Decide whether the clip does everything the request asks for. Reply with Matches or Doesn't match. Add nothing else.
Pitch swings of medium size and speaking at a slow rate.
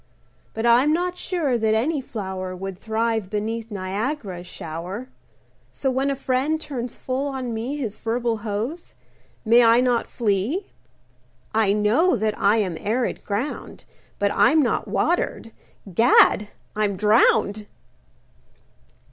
Matches